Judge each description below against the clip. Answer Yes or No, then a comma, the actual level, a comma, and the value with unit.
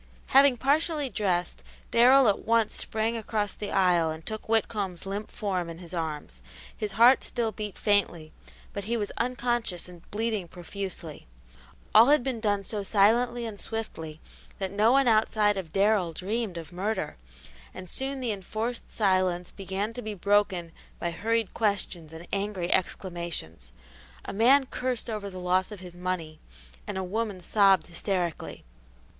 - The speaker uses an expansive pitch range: No, average, 3.9 semitones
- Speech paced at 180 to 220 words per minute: No, average, 155 wpm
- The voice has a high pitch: Yes, high, 200 Hz